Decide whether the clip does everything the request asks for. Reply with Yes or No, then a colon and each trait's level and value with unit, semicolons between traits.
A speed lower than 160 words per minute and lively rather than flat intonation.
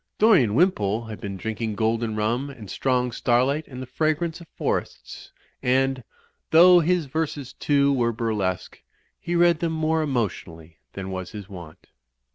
Yes: average, 150 wpm; wide, 6.5 semitones